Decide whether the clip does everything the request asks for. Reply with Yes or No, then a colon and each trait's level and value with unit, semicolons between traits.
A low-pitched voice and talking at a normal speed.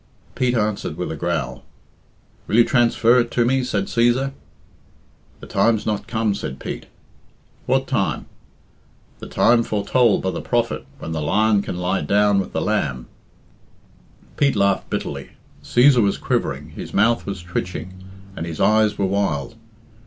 Yes: low, 105 Hz; average, 155 wpm